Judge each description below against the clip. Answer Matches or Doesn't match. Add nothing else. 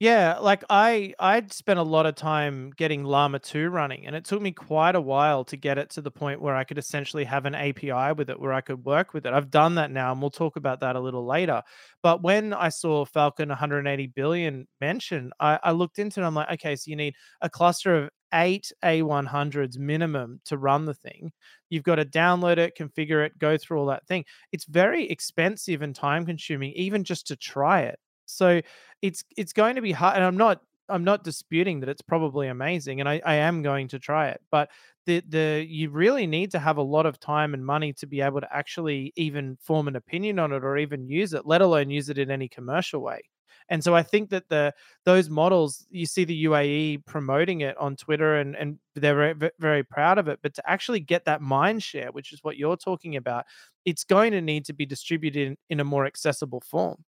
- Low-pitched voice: Doesn't match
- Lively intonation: Doesn't match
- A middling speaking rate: Doesn't match